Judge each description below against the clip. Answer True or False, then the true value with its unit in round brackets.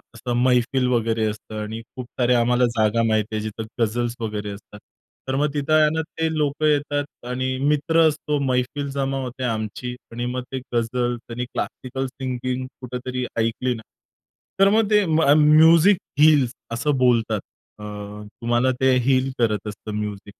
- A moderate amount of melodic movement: True (3.6 semitones)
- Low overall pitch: True (125 Hz)